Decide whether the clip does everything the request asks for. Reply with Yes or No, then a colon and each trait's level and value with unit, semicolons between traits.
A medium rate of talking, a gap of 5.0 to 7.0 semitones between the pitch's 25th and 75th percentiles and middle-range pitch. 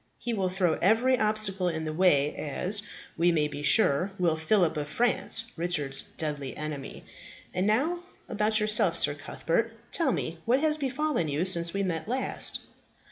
Yes: average, 165 wpm; wide, 5.6 semitones; medium, 180 Hz